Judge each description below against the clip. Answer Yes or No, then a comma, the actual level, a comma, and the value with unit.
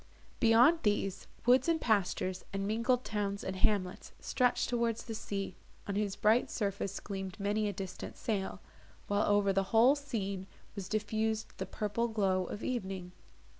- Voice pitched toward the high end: Yes, high, 205 Hz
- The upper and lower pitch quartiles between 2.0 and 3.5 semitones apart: Yes, average, 2.7 semitones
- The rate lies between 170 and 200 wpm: No, average, 155 wpm